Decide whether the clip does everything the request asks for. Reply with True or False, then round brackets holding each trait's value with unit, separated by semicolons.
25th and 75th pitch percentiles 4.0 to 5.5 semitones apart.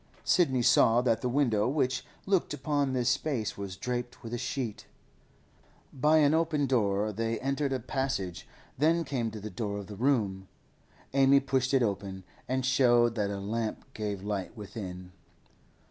True (4.6 semitones)